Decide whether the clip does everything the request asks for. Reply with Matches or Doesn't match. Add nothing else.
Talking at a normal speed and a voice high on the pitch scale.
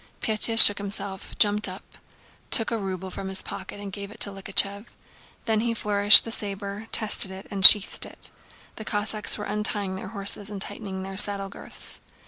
Matches